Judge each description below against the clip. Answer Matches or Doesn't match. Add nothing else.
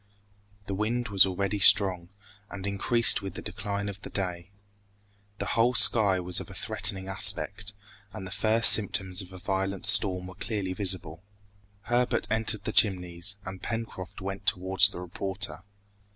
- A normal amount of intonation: Doesn't match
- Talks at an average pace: Matches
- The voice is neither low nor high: Doesn't match